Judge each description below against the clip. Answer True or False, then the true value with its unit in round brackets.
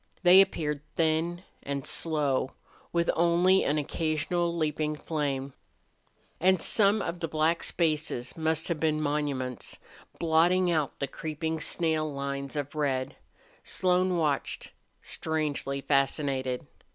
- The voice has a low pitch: False (155 Hz)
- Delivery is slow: True (115 wpm)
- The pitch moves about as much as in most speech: True (3.1 semitones)